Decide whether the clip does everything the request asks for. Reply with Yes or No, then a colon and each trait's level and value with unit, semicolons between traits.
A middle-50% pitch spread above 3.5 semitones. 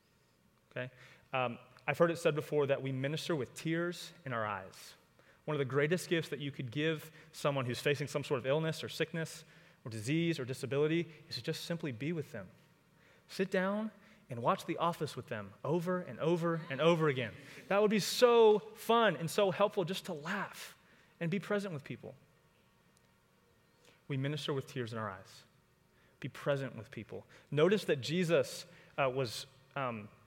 Yes: average, 4.4 semitones